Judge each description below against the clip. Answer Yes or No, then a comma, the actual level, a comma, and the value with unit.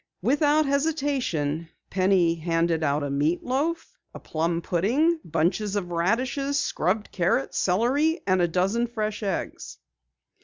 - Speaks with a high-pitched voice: Yes, high, 195 Hz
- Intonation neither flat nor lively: No, wide, 8.2 semitones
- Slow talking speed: Yes, slow, 125 wpm